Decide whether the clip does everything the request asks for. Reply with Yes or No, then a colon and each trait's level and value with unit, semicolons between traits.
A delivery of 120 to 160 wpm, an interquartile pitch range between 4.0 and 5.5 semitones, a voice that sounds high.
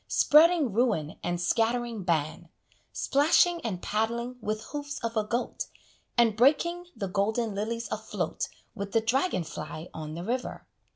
Yes: average, 140 wpm; average, 4.4 semitones; high, 225 Hz